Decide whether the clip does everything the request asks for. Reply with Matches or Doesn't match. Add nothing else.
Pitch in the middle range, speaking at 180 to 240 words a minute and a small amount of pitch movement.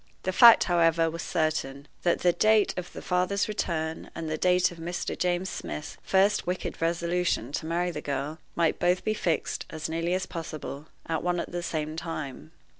Matches